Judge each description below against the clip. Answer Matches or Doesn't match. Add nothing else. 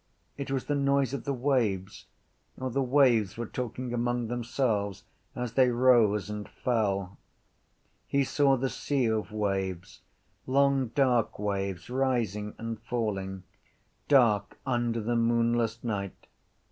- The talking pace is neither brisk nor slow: Doesn't match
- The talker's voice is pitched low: Matches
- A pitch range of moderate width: Matches